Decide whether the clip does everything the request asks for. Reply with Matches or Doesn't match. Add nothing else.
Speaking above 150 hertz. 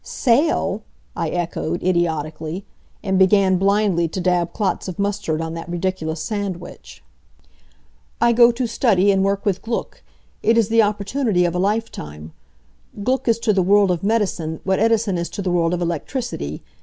Matches